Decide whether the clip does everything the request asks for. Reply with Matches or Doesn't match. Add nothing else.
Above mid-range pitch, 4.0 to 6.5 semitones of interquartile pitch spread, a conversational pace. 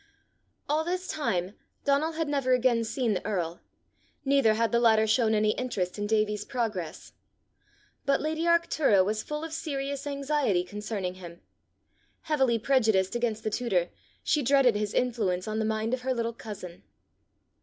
Matches